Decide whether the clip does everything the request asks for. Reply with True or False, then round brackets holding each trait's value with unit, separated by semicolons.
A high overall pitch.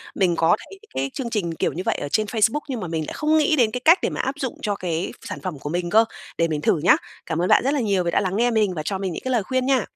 True (200 Hz)